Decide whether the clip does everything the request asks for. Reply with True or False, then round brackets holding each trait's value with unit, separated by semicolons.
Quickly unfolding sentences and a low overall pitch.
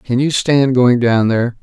True (220 wpm; 125 Hz)